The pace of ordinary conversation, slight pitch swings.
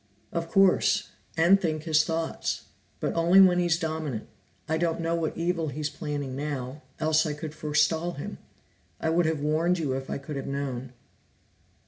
Yes: average, 170 wpm; narrow, 2.2 semitones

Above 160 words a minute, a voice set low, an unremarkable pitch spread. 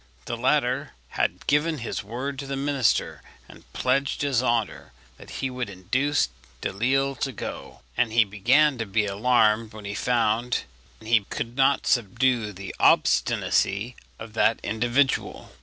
No: average, 145 wpm; low, 120 Hz; average, 3.8 semitones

